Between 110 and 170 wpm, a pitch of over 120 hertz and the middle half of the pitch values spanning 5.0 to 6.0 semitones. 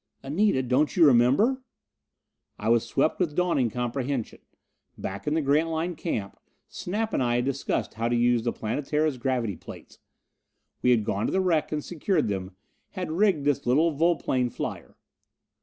Yes: average, 160 wpm; medium, 140 Hz; average, 5.3 semitones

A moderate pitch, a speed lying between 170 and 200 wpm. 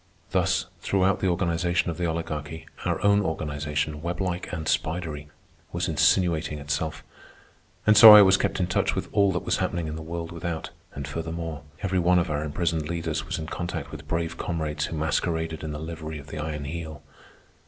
No: very low, 80 Hz; average, 185 wpm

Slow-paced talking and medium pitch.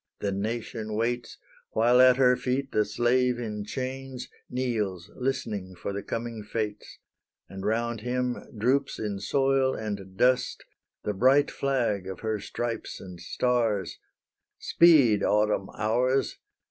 No: slow, 130 wpm; low, 115 Hz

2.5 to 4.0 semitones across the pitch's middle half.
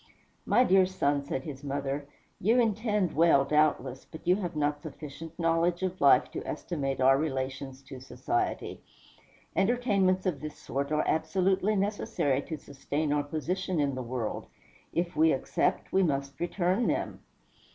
No: average, 5.0 semitones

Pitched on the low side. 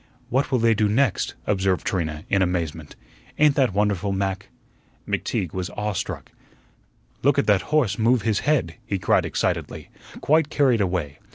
Yes: low, 100 Hz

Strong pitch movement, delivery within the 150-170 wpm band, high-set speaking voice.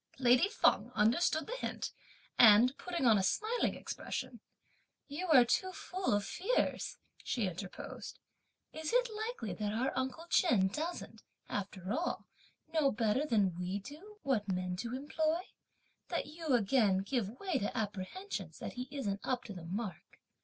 Yes: wide, 7.9 semitones; average, 155 wpm; high, 245 Hz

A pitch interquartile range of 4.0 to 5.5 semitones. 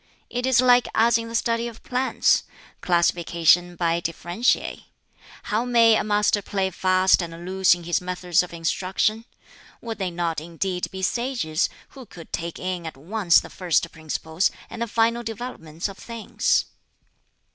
Yes: average, 5.1 semitones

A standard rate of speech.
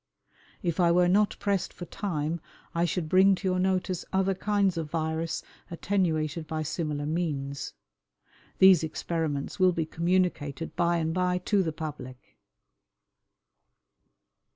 No: slow, 130 wpm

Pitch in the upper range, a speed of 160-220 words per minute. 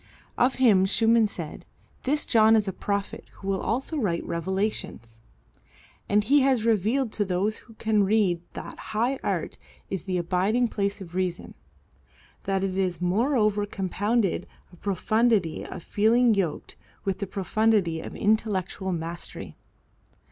No: high, 205 Hz; average, 140 wpm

